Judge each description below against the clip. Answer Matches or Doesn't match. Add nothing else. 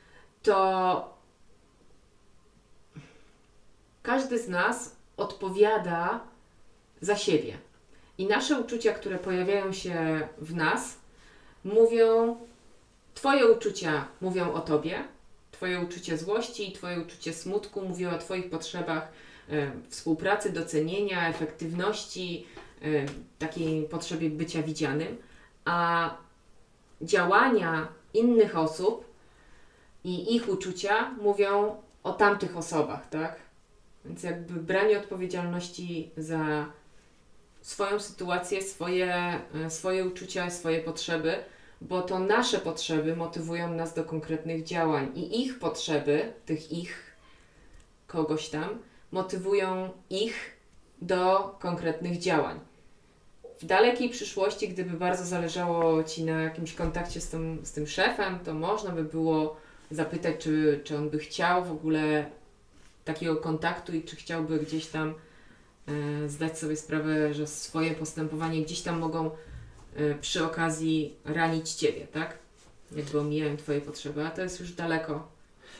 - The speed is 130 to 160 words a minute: Doesn't match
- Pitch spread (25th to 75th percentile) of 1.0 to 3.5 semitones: Matches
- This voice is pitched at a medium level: Matches